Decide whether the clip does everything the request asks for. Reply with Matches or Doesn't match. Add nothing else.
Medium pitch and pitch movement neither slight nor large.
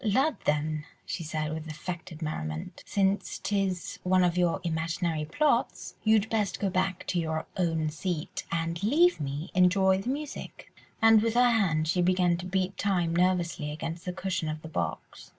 Matches